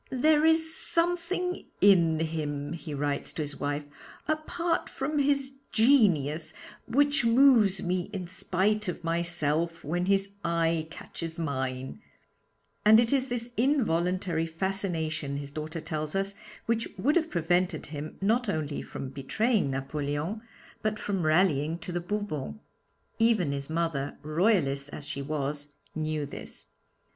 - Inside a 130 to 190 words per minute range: Yes, slow, 135 wpm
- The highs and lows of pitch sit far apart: Yes, wide, 6.4 semitones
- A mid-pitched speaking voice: Yes, medium, 170 Hz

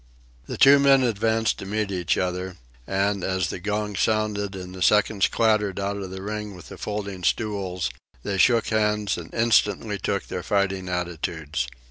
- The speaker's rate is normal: Yes, average, 170 wpm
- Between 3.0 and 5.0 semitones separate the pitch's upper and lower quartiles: No, narrow, 2.4 semitones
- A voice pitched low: Yes, low, 100 Hz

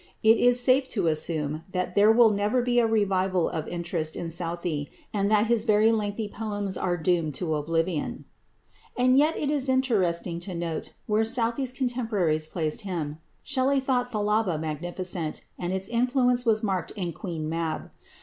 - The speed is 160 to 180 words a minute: Yes, average, 165 wpm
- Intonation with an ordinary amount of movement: No, wide, 5.8 semitones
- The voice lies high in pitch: Yes, high, 200 Hz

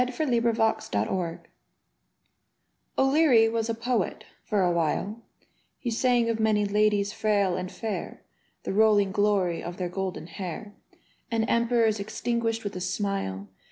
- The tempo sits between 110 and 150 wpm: Yes, average, 140 wpm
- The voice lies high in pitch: Yes, high, 210 Hz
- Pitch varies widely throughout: No, average, 3.3 semitones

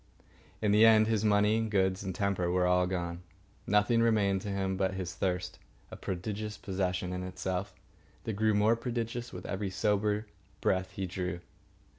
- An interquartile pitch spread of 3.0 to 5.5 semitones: No, narrow, 2.5 semitones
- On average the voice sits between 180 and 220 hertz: No, low, 100 Hz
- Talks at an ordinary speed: Yes, average, 170 wpm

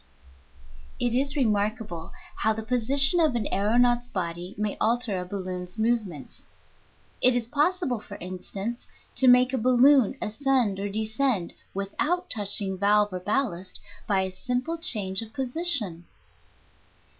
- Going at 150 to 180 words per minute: No, slow, 135 wpm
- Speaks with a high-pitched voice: Yes, high, 220 Hz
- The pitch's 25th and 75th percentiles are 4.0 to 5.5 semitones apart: Yes, average, 4.5 semitones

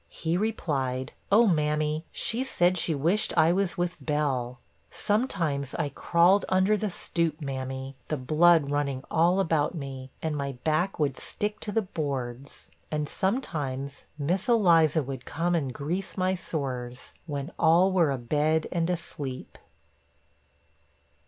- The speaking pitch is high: No, medium, 155 Hz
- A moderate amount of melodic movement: Yes, average, 4.4 semitones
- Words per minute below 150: Yes, average, 140 wpm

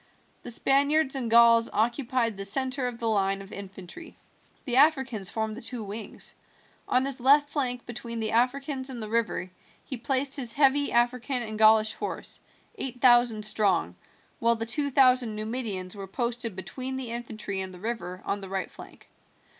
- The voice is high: Yes, high, 235 Hz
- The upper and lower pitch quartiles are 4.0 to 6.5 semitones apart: No, average, 3.4 semitones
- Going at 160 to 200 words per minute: Yes, average, 170 wpm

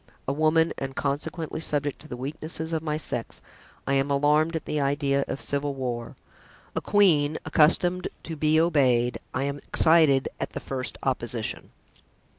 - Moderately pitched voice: Yes, medium, 145 Hz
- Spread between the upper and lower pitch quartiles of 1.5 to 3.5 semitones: Yes, narrow, 2.6 semitones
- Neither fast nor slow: Yes, average, 160 wpm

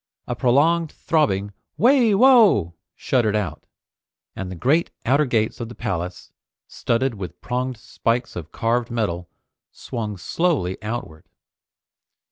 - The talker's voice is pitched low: Yes, low, 115 Hz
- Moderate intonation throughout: No, wide, 6.6 semitones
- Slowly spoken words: Yes, slow, 120 wpm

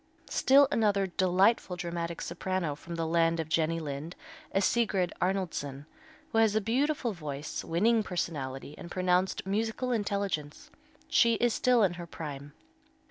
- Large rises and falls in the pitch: No, average, 4.7 semitones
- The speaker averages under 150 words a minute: Yes, average, 140 wpm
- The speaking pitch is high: No, medium, 180 Hz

